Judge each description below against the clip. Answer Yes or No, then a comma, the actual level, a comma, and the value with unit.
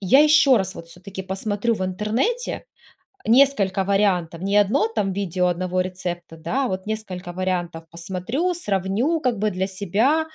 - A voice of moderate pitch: No, high, 195 Hz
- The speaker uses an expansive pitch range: No, average, 3.7 semitones